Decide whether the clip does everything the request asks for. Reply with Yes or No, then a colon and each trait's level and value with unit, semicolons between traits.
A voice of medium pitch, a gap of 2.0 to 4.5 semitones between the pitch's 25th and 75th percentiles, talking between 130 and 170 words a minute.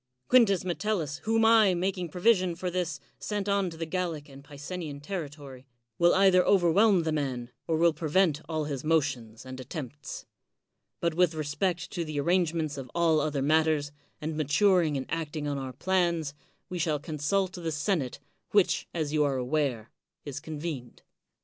Yes: medium, 160 Hz; average, 3.8 semitones; average, 165 wpm